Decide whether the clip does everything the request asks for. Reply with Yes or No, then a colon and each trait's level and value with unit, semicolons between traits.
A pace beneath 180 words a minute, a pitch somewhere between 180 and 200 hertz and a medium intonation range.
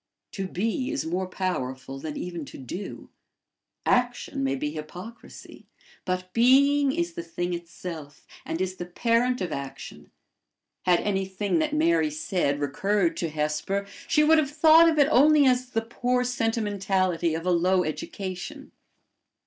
No: average, 150 wpm; high, 190 Hz; wide, 6.8 semitones